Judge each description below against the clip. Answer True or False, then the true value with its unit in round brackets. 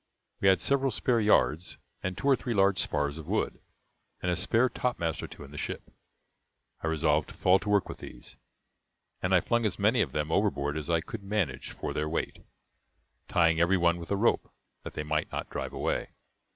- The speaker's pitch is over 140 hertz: False (90 Hz)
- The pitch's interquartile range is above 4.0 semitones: True (5.0 semitones)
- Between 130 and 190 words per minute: False (205 wpm)